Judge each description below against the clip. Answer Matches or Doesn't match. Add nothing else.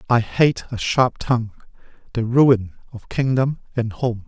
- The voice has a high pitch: Doesn't match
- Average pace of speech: Matches